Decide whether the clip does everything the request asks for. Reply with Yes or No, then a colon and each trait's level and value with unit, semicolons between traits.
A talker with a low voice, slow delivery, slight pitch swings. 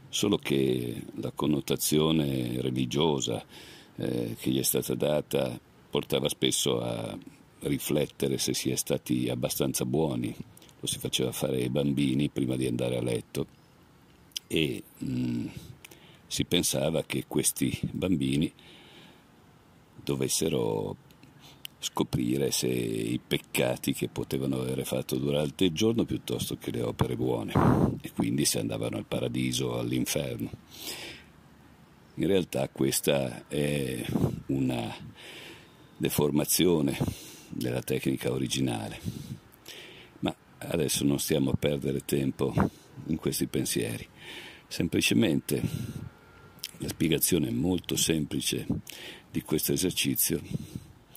Yes: very low, 65 Hz; slow, 105 wpm; narrow, 2.2 semitones